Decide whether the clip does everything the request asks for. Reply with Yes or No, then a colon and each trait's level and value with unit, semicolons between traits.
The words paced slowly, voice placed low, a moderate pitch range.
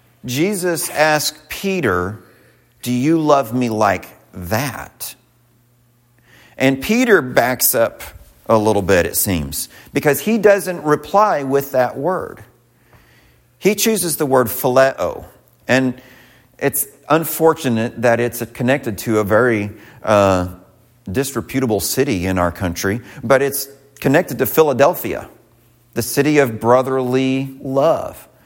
Yes: slow, 115 wpm; low, 125 Hz; average, 3.5 semitones